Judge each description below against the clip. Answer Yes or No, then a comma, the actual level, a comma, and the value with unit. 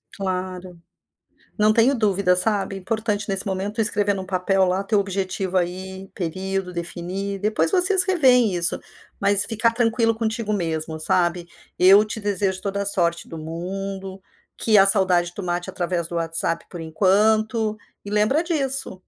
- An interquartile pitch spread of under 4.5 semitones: Yes, average, 2.9 semitones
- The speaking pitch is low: No, high, 195 Hz